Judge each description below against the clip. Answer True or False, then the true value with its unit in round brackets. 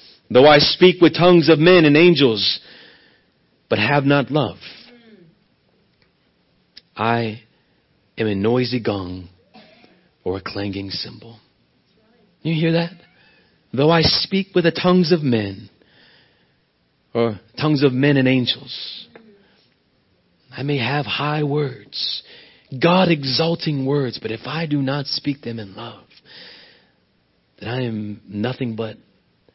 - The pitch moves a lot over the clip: True (6.7 semitones)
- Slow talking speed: True (125 wpm)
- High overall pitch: False (135 Hz)